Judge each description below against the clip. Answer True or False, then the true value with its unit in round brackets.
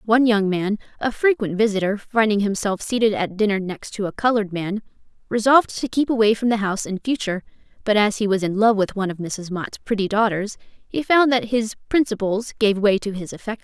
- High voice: True (210 Hz)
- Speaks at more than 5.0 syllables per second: True (5.8 syllables/s)